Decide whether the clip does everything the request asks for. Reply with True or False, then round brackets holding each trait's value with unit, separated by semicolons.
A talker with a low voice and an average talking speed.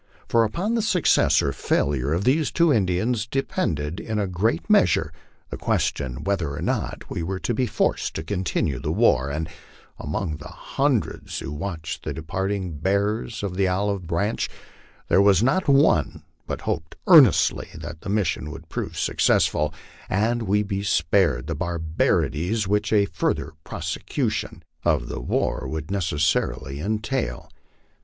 True (95 Hz; 155 wpm)